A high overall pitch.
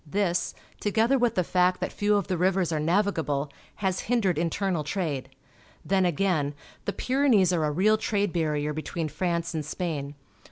No: medium, 180 Hz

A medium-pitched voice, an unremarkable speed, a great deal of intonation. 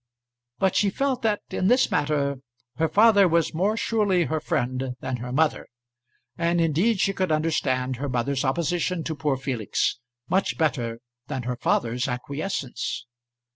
Yes: medium, 155 Hz; average, 150 wpm; wide, 6.2 semitones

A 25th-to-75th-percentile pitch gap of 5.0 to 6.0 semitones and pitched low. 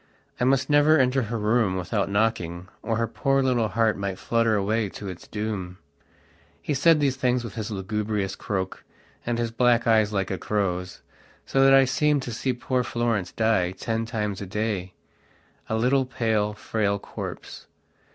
No: average, 3.7 semitones; low, 110 Hz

